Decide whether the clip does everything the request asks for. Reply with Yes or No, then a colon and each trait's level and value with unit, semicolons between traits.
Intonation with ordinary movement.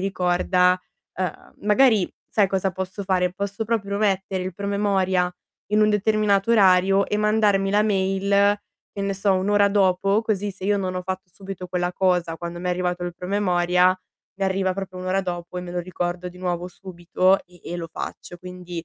No: narrow, 1.9 semitones